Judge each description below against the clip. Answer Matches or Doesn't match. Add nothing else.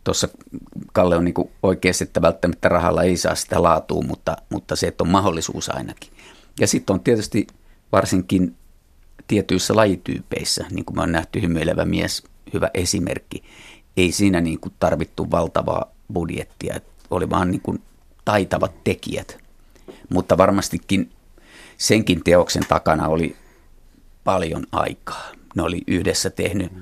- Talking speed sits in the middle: Matches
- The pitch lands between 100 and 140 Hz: Doesn't match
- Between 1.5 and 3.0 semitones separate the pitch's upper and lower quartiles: Matches